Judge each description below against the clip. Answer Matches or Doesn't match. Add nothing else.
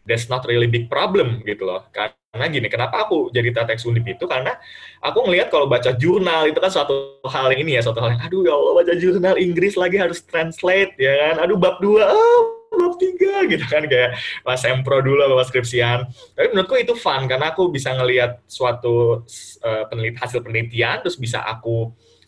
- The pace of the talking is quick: Matches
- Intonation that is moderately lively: Doesn't match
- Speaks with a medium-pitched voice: Doesn't match